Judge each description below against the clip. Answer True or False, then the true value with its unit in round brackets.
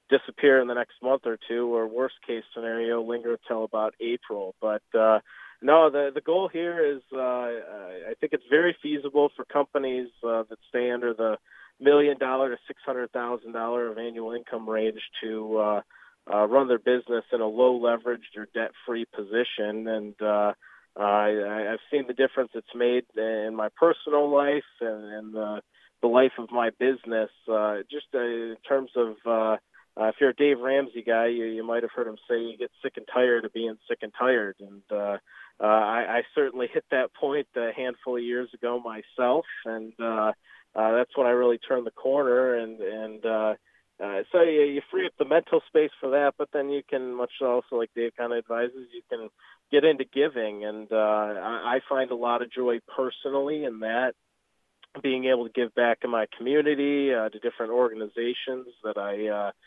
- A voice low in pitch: True (120 Hz)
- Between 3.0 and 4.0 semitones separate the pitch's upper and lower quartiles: True (3.3 semitones)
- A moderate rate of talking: True (195 wpm)